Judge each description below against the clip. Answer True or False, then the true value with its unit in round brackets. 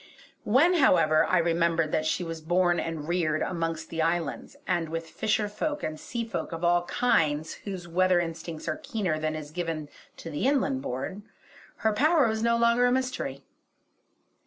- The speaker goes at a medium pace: True (175 wpm)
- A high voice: False (175 Hz)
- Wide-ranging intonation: True (5.8 semitones)